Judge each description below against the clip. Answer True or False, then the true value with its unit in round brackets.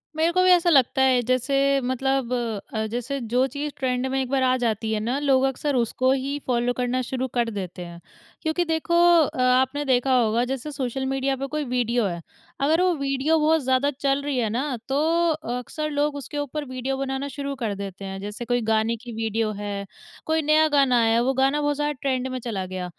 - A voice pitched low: False (260 Hz)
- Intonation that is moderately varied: True (3.0 semitones)